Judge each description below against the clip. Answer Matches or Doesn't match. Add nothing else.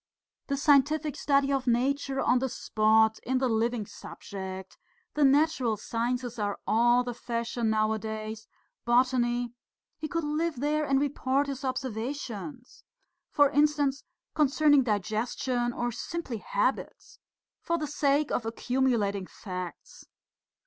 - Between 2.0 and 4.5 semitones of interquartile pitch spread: Matches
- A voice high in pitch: Matches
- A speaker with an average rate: Doesn't match